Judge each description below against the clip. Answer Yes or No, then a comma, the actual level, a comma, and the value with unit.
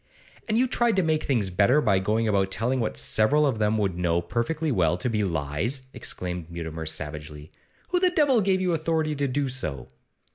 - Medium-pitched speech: No, low, 110 Hz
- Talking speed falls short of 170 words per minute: No, average, 195 wpm